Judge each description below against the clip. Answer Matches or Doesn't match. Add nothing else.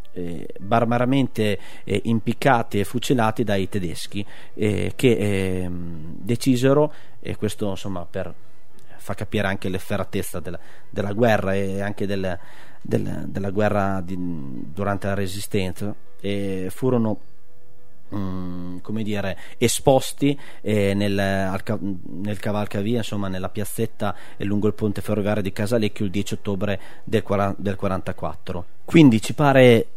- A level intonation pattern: Matches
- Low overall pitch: Matches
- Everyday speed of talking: Matches